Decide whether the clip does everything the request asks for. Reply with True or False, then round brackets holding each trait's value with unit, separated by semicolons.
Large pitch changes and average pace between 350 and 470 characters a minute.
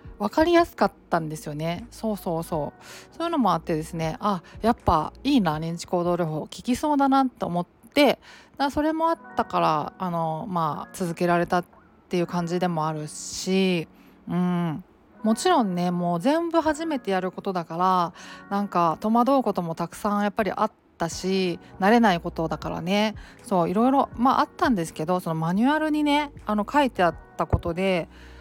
True (6.0 semitones; 360 characters per minute)